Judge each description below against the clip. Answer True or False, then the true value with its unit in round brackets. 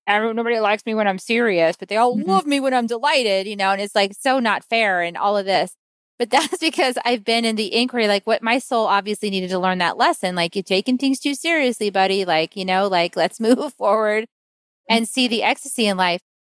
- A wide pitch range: False (4.0 semitones)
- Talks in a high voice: True (220 Hz)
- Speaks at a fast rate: True (235 wpm)